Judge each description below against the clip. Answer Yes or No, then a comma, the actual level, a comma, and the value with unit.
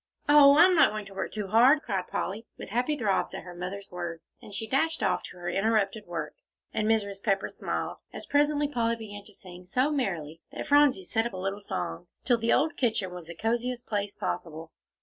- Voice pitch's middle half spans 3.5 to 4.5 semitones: No, average, 5.1 semitones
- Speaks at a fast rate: Yes, fast, 210 wpm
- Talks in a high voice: Yes, high, 210 Hz